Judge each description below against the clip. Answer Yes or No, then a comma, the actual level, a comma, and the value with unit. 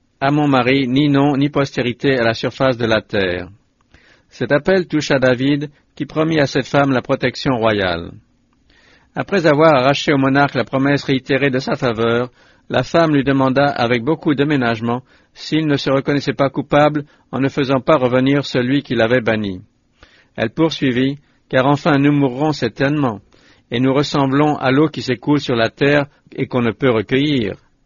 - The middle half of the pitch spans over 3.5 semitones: No, narrow, 2.6 semitones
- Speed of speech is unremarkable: Yes, average, 175 wpm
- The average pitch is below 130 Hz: No, low, 135 Hz